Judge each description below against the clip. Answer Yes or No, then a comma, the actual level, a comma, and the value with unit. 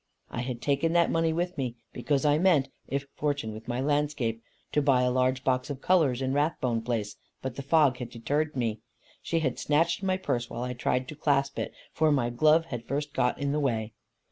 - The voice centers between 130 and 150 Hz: Yes, medium, 140 Hz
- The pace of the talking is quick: Yes, fast, 215 wpm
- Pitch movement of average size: Yes, average, 3.4 semitones